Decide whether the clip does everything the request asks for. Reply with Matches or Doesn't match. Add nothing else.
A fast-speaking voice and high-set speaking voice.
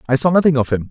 Doesn't match